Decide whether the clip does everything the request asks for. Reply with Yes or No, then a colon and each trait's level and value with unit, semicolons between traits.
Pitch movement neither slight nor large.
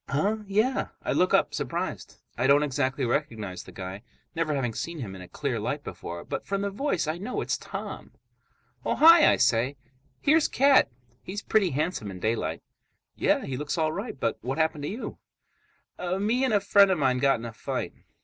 No: wide, 8.5 semitones